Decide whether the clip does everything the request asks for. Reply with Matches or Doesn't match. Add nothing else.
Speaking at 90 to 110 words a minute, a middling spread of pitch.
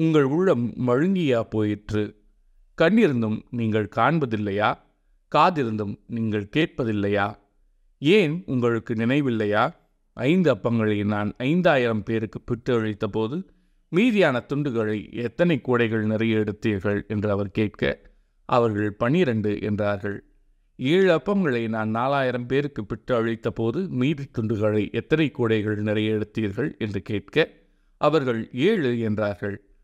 Matches